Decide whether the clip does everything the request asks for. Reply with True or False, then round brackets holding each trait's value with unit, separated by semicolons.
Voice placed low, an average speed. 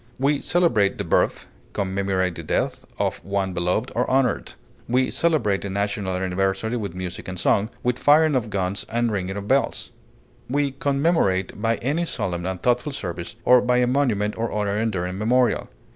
True (105 Hz; 170 wpm)